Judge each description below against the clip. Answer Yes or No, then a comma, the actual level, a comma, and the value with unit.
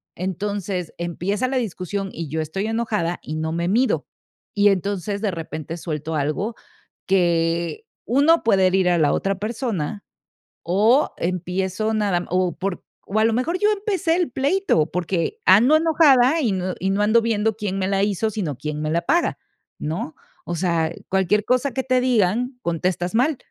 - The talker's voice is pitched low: No, high, 195 Hz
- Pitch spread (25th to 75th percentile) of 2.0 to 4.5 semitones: No, average, 5.3 semitones